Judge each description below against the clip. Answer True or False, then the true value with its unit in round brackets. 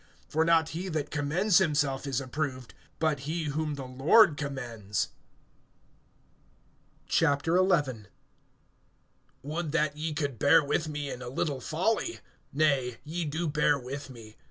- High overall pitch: False (150 Hz)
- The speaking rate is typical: False (130 wpm)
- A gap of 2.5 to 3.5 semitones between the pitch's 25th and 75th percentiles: True (3.0 semitones)